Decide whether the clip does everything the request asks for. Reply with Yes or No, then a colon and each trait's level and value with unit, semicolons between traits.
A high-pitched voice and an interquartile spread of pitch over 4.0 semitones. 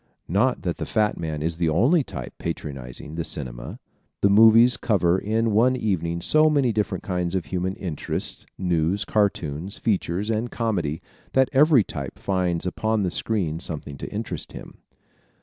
No: very low, 95 Hz; average, 5.3 semitones